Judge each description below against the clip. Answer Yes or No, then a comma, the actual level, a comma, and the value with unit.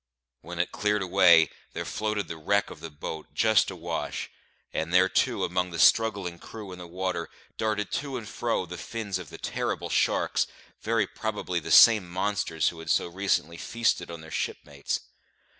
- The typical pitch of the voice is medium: No, very low, 90 Hz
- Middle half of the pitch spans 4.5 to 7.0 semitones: No, average, 3.7 semitones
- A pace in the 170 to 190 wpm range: Yes, average, 175 wpm